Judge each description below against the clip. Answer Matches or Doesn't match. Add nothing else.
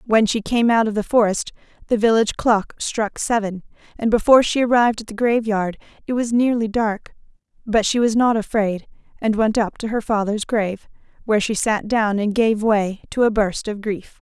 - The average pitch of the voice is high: Matches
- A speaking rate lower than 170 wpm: Doesn't match